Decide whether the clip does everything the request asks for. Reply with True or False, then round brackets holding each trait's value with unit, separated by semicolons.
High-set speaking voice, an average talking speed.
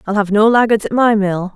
False (210 Hz; 270 wpm)